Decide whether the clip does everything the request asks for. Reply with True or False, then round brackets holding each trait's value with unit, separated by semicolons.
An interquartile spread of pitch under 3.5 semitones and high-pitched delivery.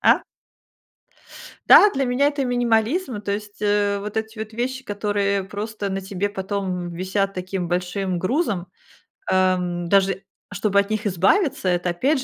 True (2.9 semitones; 200 Hz)